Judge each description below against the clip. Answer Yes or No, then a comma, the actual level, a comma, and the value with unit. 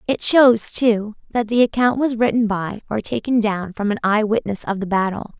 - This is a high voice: Yes, high, 220 Hz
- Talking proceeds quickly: Yes, fast, 210 wpm